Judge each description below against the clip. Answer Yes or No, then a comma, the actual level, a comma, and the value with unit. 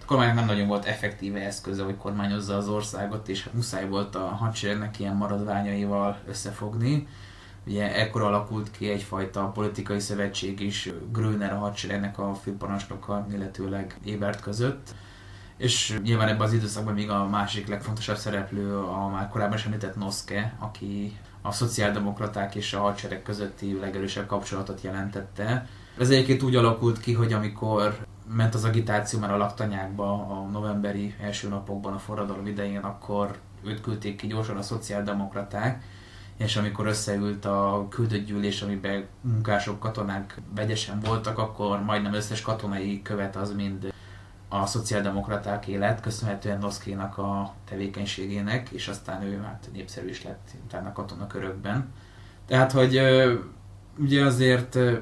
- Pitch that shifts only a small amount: Yes, narrow, 1.4 semitones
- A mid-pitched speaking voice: No, low, 100 Hz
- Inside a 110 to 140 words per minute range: Yes, average, 135 wpm